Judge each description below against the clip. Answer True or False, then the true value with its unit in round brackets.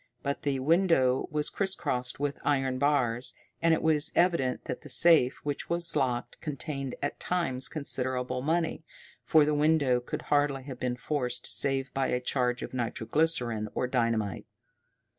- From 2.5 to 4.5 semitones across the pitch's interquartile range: True (3.3 semitones)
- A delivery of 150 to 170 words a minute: True (160 wpm)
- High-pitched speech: False (135 Hz)